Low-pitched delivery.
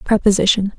No: high, 200 Hz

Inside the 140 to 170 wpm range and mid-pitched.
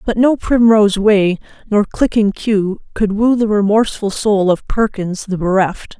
No: average, 160 wpm; high, 210 Hz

